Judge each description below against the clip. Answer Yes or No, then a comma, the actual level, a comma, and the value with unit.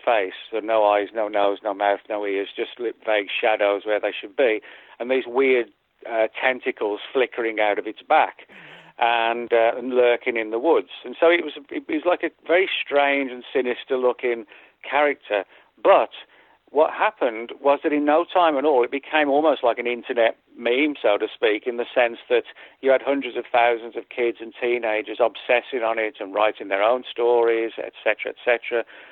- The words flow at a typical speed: Yes, average, 185 wpm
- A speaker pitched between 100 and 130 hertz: Yes, low, 120 Hz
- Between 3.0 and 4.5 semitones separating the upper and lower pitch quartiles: Yes, average, 4.2 semitones